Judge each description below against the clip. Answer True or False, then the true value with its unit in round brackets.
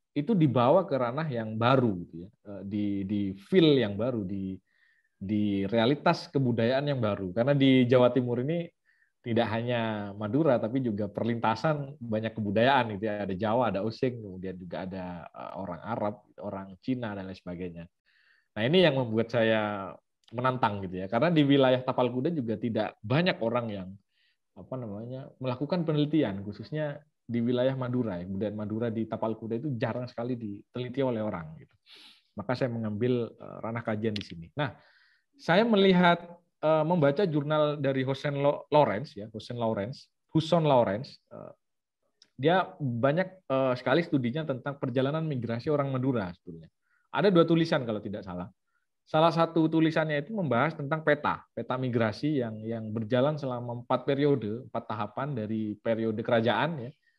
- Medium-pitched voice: False (120 Hz)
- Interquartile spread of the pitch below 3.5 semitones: False (5.2 semitones)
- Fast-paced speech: True (150 wpm)